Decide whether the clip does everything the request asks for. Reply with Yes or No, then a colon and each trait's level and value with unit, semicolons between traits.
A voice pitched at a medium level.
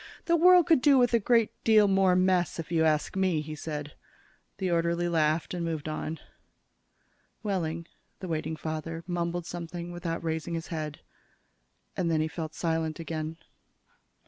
Yes: medium, 170 Hz